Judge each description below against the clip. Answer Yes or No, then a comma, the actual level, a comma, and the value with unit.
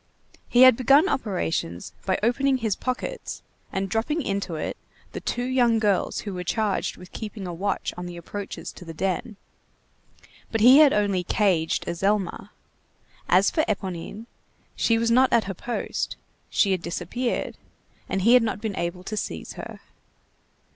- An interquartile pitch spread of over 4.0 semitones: Yes, average, 4.5 semitones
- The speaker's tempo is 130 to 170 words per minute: Yes, average, 160 wpm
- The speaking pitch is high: Yes, high, 205 Hz